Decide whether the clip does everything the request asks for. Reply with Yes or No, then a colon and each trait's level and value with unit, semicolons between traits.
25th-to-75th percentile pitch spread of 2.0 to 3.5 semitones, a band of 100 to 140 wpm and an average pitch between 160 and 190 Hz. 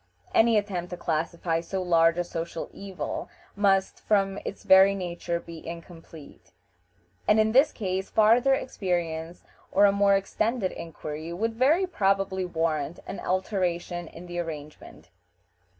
Yes: average, 3.1 semitones; slow, 135 wpm; medium, 185 Hz